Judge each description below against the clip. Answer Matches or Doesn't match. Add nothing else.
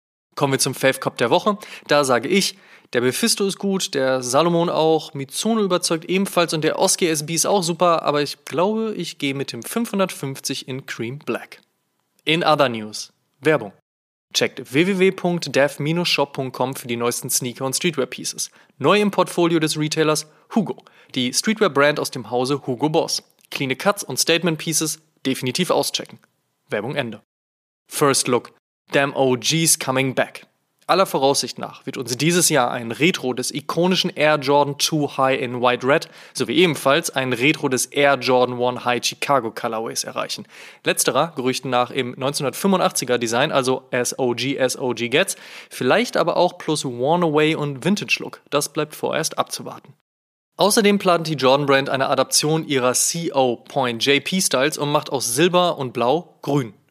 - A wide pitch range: Doesn't match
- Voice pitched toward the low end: Doesn't match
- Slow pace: Doesn't match